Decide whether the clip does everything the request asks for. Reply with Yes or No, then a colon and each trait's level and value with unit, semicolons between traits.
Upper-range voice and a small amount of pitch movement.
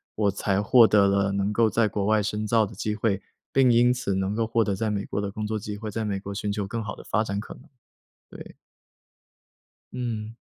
No: low, 105 Hz; narrow, 1.9 semitones